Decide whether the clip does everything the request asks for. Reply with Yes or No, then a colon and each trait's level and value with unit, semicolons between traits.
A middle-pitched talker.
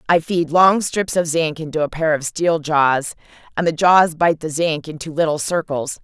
Yes: medium, 160 Hz